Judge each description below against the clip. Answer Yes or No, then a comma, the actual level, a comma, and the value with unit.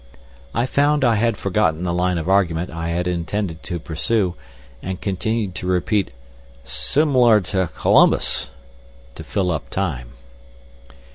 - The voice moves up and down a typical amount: Yes, average, 3.9 semitones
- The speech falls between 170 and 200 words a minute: No, slow, 135 wpm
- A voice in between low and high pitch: No, very low, 95 Hz